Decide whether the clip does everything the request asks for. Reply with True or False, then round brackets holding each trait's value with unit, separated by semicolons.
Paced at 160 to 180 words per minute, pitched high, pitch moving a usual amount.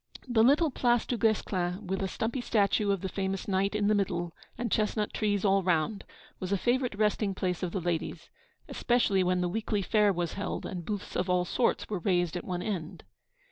False (205 wpm; 195 Hz; 3.0 semitones)